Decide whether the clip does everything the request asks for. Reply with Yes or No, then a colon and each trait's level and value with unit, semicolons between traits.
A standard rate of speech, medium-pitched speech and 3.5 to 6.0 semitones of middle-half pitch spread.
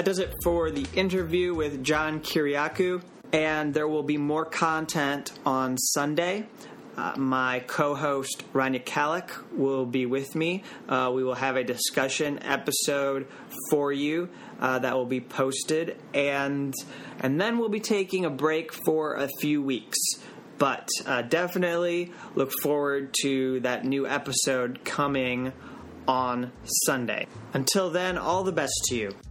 Yes: average, 145 wpm; medium, 145 Hz; average, 3.8 semitones